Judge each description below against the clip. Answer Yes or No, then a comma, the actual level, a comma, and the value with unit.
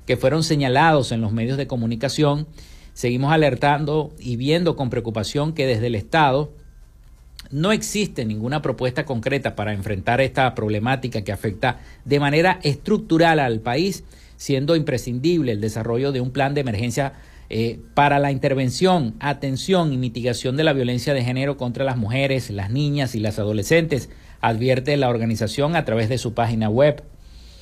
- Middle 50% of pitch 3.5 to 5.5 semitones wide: Yes, average, 3.9 semitones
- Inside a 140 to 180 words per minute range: Yes, average, 155 wpm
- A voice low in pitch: Yes, low, 130 Hz